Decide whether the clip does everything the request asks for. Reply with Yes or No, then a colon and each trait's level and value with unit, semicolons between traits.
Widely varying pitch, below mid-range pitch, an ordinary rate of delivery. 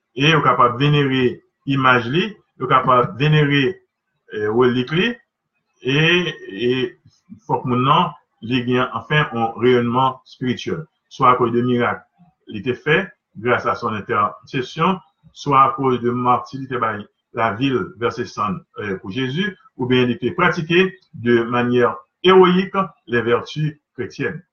No: wide, 5.7 semitones; low, 130 Hz; slow, 135 wpm